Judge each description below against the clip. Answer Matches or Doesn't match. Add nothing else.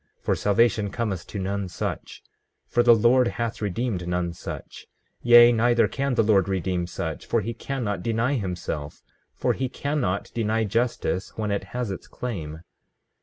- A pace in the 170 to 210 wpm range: Doesn't match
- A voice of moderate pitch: Doesn't match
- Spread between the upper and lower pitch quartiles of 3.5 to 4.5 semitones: Matches